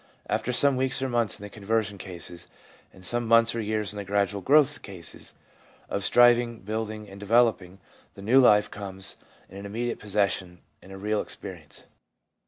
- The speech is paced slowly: No, average, 175 wpm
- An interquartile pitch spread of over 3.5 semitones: No, average, 3.2 semitones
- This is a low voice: Yes, low, 105 Hz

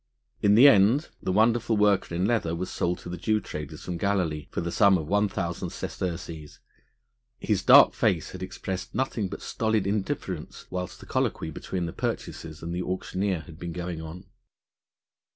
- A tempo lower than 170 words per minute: No, average, 175 wpm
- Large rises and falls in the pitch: No, average, 3.4 semitones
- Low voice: Yes, very low, 90 Hz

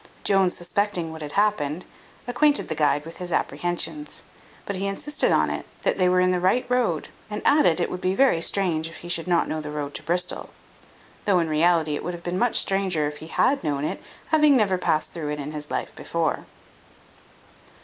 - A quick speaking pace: Yes, fast, 210 wpm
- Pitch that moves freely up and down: No, average, 4.0 semitones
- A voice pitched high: No, medium, 175 Hz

